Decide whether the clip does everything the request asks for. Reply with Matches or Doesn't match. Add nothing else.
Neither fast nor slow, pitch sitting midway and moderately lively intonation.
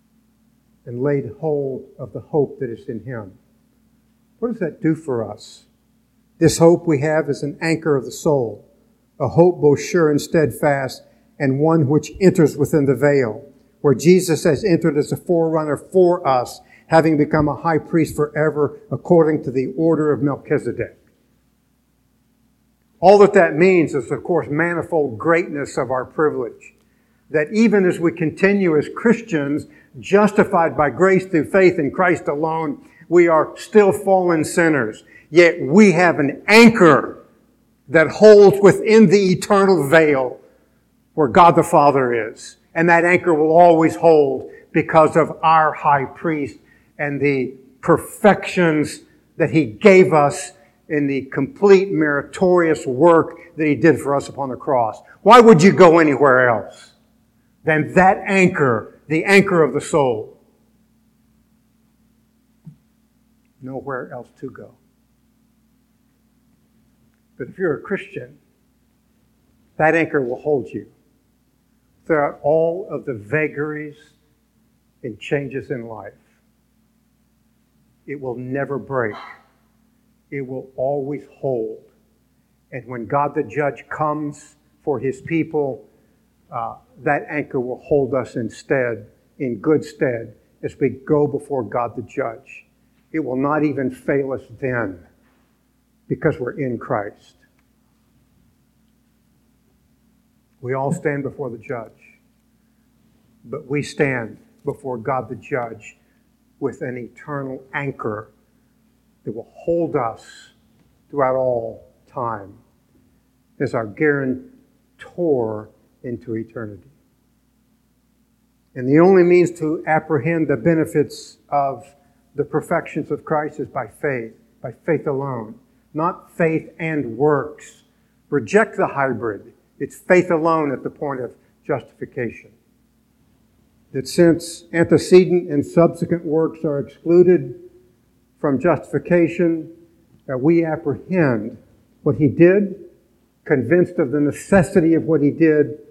Doesn't match